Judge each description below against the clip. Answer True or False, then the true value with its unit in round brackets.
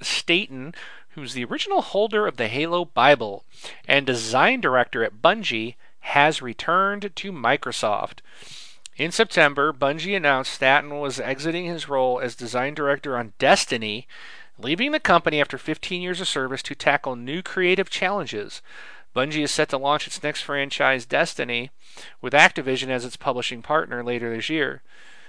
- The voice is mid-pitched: True (145 Hz)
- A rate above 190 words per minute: False (150 wpm)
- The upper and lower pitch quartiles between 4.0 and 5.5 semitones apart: True (5.1 semitones)